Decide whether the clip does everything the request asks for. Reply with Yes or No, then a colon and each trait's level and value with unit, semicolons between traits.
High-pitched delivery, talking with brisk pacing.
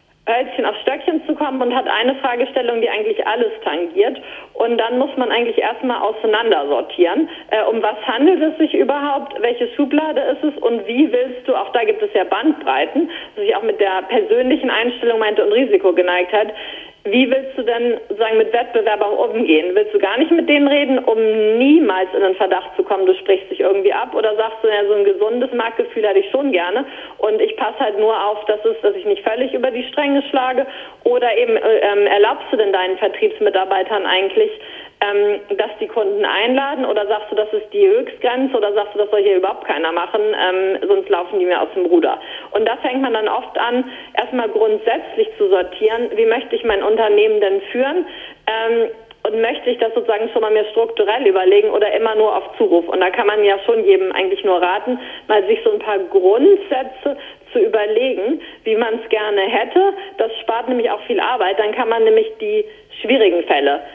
Yes: very high, 255 Hz; fast, 205 wpm